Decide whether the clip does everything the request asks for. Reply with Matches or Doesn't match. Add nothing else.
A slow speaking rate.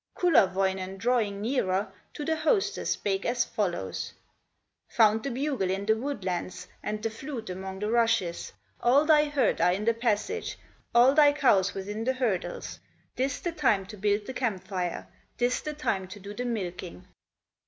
Doesn't match